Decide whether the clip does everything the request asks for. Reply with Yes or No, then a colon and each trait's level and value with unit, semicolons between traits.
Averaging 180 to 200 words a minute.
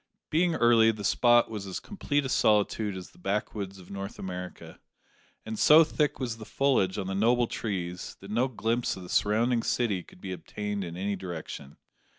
Yes: average, 185 wpm